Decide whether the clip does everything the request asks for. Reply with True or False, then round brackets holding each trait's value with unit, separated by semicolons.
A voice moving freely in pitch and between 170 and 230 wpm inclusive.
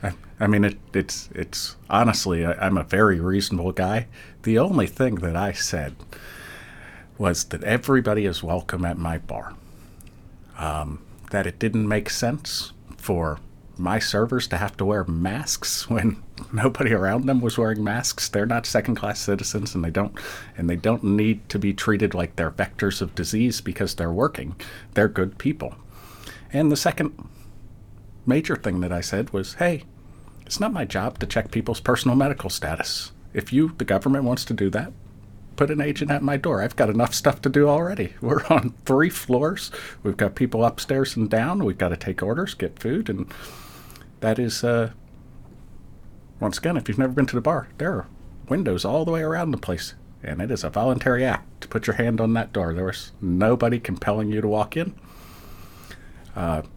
False (4.8 semitones; 180 wpm)